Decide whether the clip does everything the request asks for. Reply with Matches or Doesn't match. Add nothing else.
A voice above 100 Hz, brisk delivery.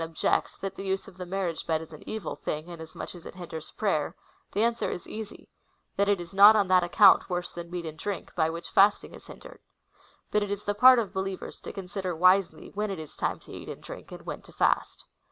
Matches